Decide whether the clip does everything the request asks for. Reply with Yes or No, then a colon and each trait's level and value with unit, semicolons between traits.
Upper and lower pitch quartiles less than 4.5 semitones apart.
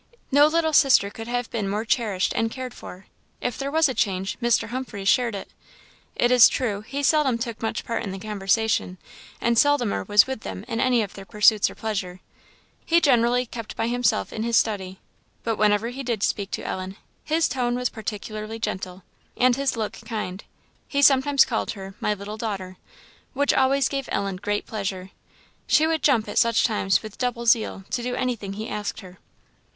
Yes: average, 3.6 semitones